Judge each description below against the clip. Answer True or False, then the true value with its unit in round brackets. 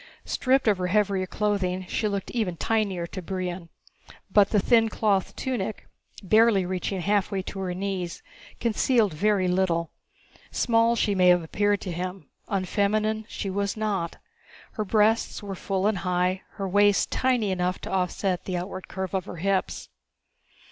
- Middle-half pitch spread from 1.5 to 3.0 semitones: True (2.5 semitones)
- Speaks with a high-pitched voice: True (195 Hz)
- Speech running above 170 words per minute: False (155 wpm)